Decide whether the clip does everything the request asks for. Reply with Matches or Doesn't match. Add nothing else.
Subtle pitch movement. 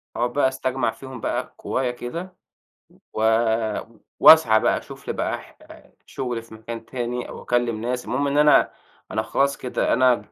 Matches